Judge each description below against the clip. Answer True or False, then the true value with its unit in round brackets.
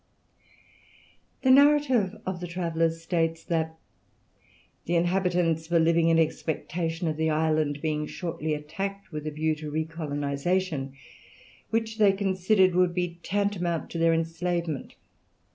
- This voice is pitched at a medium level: True (165 Hz)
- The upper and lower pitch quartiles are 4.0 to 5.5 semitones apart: False (2.6 semitones)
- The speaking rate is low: True (125 wpm)